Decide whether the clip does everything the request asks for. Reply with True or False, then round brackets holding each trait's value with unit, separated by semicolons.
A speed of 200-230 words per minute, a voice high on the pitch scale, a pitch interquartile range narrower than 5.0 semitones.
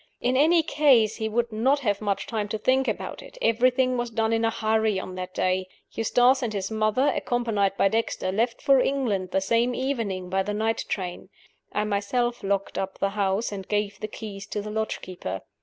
True (205 wpm; 220 Hz; 3.6 semitones)